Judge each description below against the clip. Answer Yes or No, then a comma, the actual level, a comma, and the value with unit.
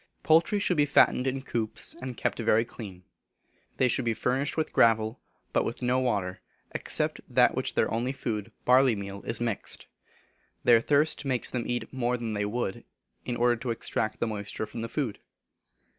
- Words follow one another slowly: No, average, 185 wpm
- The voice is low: Yes, low, 120 Hz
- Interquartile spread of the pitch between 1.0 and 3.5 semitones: Yes, average, 2.8 semitones